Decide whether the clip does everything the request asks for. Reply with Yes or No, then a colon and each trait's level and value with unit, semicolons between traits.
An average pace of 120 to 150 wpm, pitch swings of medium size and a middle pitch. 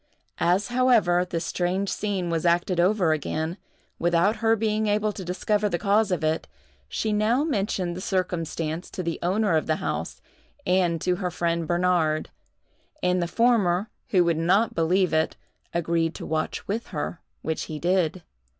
No: average, 165 wpm; average, 3.5 semitones; medium, 180 Hz